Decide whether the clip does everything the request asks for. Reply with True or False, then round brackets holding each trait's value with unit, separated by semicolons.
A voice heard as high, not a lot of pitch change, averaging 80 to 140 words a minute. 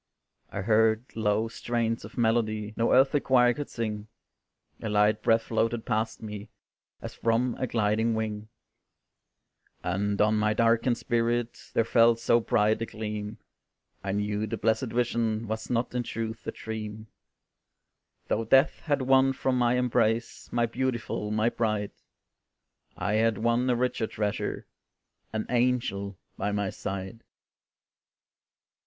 False (115 Hz; 1.8 semitones; 135 wpm)